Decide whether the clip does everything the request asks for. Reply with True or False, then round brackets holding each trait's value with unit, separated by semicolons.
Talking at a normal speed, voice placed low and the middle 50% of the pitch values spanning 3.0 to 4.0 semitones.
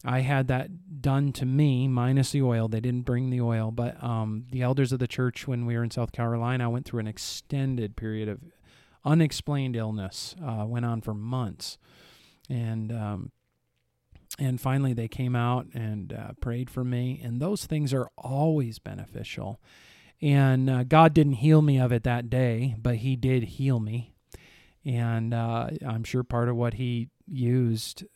False (175 wpm; 125 Hz; 2.4 semitones)